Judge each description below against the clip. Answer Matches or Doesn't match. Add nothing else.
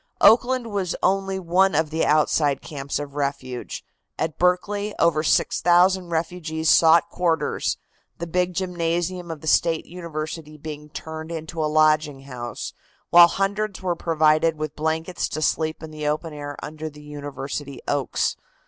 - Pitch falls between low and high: Matches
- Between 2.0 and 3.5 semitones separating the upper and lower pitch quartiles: Matches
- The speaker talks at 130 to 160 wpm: Matches